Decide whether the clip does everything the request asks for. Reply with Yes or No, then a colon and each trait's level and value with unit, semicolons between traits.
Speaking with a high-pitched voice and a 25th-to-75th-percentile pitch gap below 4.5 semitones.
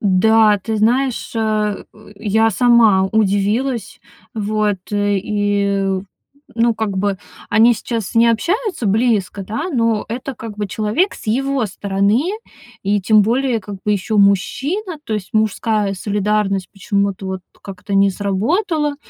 Yes: high, 215 Hz; average, 2.7 semitones